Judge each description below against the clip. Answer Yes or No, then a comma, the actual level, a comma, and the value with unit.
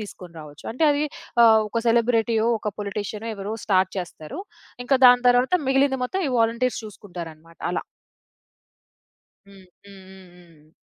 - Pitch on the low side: No, high, 210 Hz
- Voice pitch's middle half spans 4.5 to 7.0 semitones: Yes, average, 4.8 semitones